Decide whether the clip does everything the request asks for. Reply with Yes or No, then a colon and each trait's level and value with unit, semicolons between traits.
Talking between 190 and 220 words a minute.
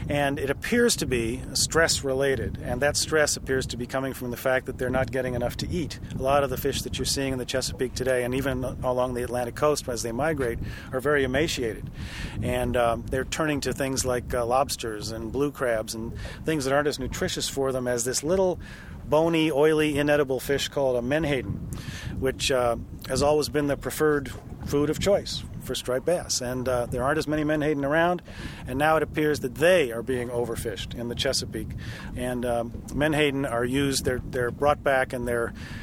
Yes: fast, 205 wpm